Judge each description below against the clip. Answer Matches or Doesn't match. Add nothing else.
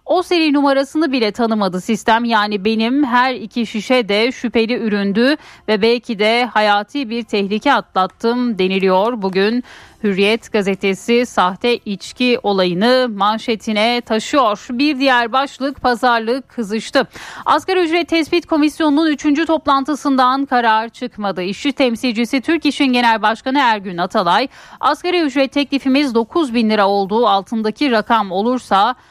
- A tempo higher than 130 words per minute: Doesn't match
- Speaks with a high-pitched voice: Matches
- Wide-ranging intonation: Doesn't match